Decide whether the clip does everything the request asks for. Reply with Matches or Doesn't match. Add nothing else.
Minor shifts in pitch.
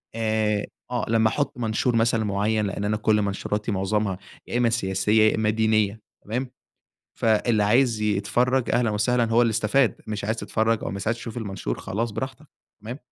Matches